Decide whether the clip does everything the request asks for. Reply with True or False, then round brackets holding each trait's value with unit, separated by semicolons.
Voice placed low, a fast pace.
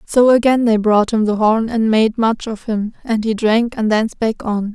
False (220 Hz; 240 wpm)